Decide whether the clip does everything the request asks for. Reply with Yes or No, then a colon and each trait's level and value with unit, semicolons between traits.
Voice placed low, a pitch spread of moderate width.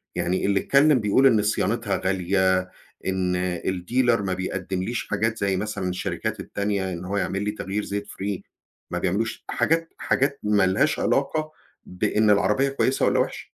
Yes: low, 100 Hz; average, 3.7 semitones